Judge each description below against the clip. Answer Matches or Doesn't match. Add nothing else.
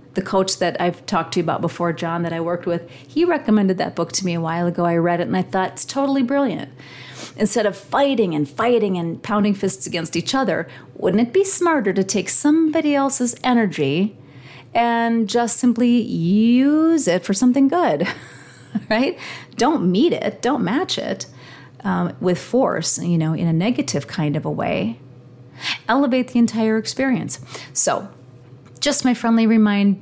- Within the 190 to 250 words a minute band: Doesn't match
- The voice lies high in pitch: Matches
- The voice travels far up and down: Matches